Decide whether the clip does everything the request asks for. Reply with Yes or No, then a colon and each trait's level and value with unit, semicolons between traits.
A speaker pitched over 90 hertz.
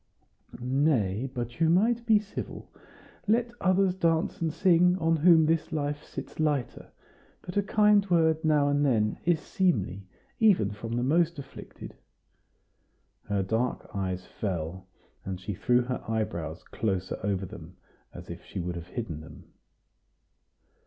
Yes: medium, 140 Hz